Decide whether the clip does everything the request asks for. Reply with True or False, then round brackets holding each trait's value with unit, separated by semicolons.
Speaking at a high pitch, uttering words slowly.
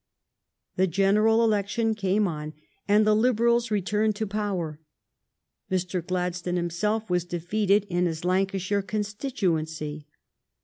True (195 Hz; 115 wpm)